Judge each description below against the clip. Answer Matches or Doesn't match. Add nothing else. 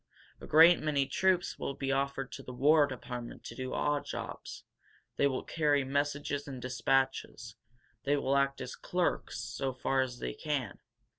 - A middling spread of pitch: Doesn't match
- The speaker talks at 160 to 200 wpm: Matches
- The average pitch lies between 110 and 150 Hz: Matches